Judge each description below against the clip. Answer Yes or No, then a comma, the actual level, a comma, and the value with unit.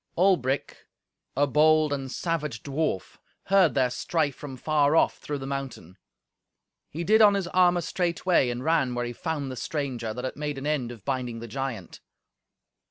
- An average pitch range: Yes, average, 4.1 semitones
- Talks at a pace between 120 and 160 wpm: No, average, 170 wpm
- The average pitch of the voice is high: No, medium, 140 Hz